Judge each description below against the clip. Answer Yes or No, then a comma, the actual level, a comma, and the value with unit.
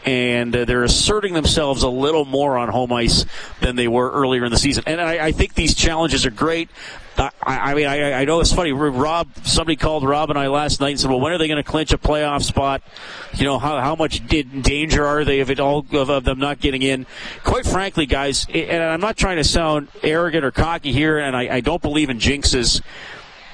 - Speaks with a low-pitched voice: No, medium, 145 Hz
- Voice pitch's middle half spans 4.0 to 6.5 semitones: No, average, 2.7 semitones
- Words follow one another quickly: Yes, fast, 230 wpm